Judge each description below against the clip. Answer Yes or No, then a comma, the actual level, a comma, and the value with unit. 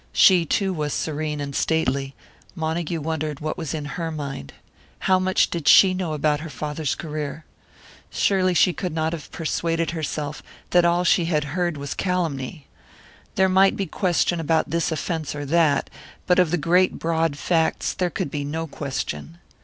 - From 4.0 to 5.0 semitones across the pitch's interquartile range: No, average, 2.8 semitones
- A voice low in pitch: No, medium, 160 Hz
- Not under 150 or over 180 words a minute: Yes, average, 175 wpm